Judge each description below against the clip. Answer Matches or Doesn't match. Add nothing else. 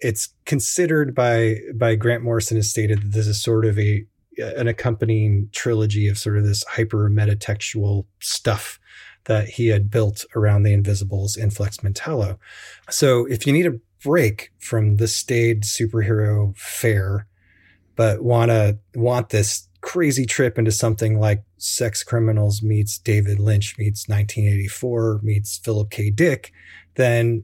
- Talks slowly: Doesn't match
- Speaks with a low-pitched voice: Matches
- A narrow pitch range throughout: Matches